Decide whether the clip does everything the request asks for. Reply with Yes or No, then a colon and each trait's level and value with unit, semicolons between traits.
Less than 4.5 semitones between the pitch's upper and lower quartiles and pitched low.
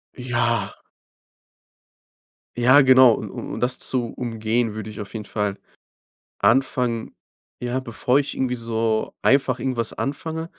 Yes: narrow, 2.6 semitones; low, 120 Hz